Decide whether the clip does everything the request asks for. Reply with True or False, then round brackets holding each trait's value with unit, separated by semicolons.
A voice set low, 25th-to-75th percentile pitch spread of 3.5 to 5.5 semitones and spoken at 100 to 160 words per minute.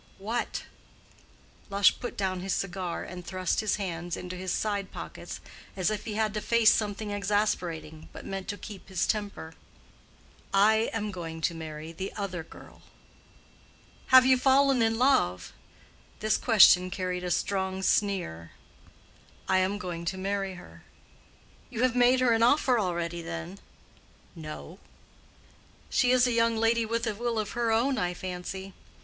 False (200 Hz; 3.9 semitones; 155 wpm)